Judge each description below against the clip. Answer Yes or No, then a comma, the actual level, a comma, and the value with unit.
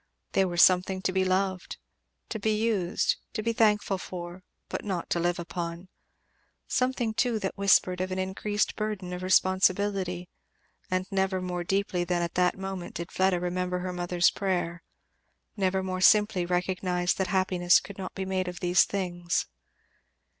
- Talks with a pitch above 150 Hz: Yes, medium, 185 Hz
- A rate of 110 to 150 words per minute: No, average, 160 wpm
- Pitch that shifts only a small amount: Yes, narrow, 1.5 semitones